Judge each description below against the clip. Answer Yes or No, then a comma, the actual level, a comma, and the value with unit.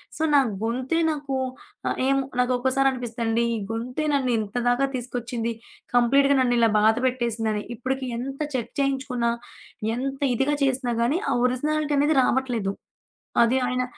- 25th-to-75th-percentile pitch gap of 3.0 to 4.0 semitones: No, narrow, 2.4 semitones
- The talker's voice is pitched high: Yes, very high, 255 Hz